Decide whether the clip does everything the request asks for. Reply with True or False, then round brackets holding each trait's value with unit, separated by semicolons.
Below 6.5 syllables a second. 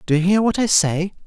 True (5.8 syllables/s)